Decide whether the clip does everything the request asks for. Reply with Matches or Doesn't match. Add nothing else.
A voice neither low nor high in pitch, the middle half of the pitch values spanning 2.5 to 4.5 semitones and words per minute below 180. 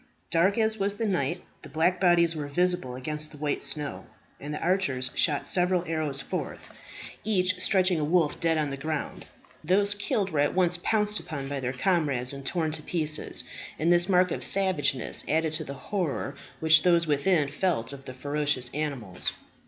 Doesn't match